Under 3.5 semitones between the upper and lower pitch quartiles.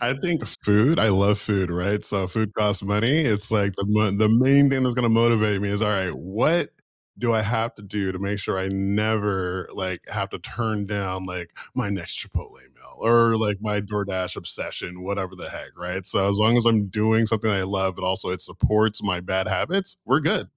Yes: average, 2.7 semitones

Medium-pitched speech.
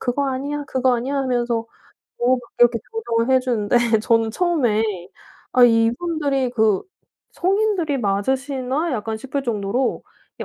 No: very high, 255 Hz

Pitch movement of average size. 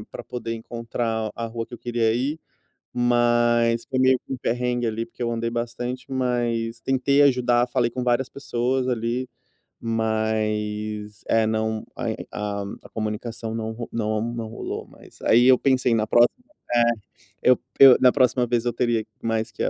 No: narrow, 1.7 semitones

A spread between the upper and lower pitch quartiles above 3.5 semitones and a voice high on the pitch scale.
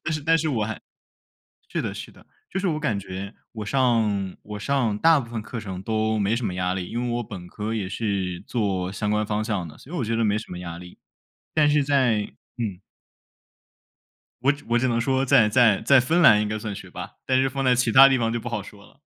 No: average, 4.2 semitones; low, 110 Hz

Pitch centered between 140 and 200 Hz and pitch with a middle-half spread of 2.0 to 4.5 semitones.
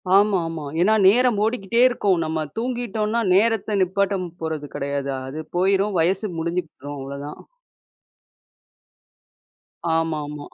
No: medium, 185 Hz; wide, 5.4 semitones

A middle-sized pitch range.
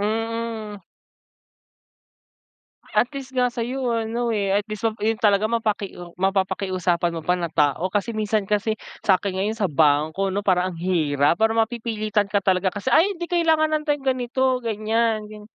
Yes: average, 3.5 semitones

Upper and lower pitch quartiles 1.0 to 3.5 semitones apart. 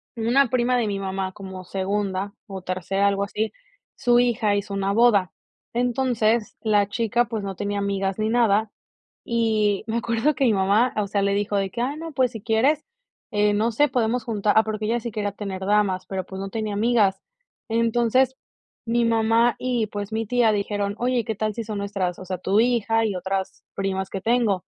Yes: average, 2.8 semitones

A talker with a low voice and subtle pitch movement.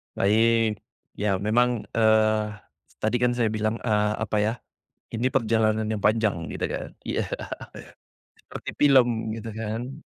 Yes: low, 110 Hz; narrow, 1.4 semitones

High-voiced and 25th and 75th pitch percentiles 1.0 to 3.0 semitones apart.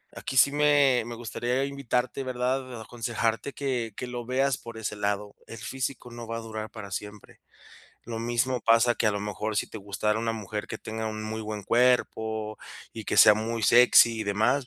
No: low, 115 Hz; narrow, 2.5 semitones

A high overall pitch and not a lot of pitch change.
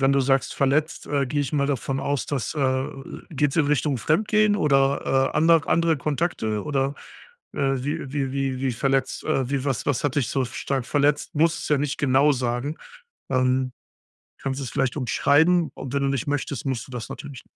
No: medium, 140 Hz; narrow, 1.9 semitones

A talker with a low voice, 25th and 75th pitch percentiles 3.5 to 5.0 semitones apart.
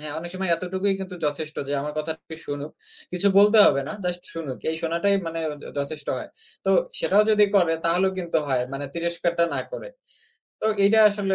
No: medium, 170 Hz; average, 3.8 semitones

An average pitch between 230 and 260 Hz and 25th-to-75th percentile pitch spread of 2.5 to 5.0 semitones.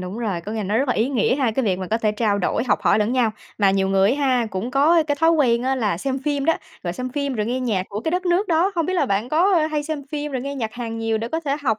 No: very high, 250 Hz; wide, 5.4 semitones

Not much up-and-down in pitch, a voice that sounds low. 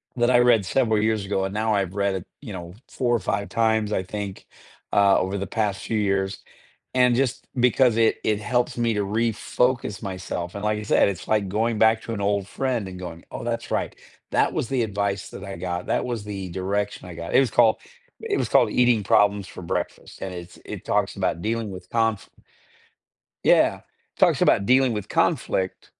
No: average, 3.1 semitones; low, 105 Hz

